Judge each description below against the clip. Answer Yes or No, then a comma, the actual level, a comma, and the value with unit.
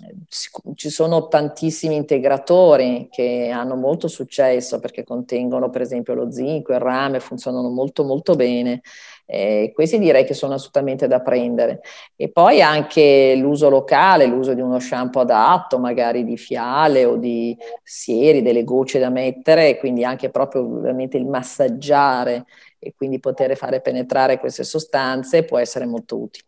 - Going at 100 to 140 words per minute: No, average, 150 wpm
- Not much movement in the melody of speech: Yes, narrow, 2.3 semitones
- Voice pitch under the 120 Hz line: No, low, 130 Hz